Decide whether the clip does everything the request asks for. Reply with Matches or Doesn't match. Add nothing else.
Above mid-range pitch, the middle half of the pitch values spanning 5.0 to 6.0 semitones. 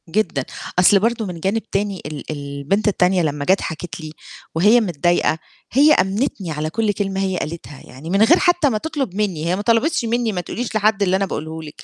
Matches